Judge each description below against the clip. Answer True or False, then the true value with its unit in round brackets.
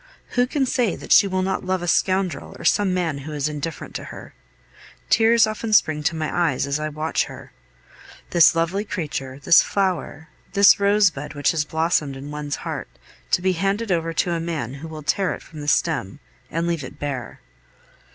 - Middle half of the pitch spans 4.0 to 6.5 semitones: True (4.3 semitones)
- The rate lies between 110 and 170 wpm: False (195 wpm)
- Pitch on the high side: False (165 Hz)